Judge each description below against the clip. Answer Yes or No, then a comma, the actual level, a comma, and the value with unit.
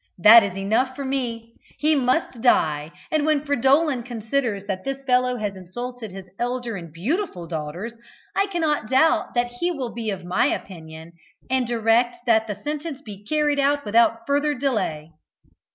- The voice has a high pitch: Yes, high, 240 Hz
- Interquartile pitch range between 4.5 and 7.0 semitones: Yes, wide, 5.5 semitones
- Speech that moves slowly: No, average, 165 wpm